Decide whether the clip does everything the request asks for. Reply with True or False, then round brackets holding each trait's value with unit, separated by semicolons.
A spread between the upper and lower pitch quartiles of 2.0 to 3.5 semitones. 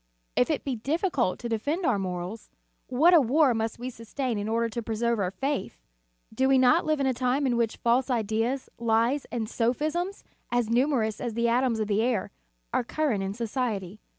True (3.2 semitones)